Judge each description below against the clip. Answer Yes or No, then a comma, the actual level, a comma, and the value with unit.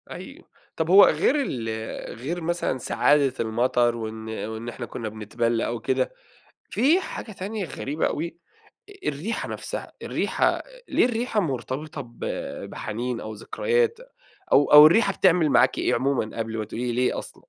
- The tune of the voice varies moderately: No, wide, 7.4 semitones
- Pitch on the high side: No, low, 135 Hz